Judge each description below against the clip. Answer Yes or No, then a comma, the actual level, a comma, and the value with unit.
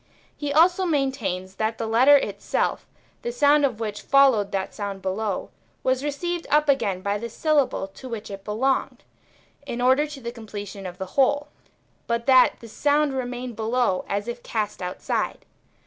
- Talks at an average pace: Yes, average, 165 wpm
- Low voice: No, high, 240 Hz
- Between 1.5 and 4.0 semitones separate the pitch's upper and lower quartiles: No, average, 5.2 semitones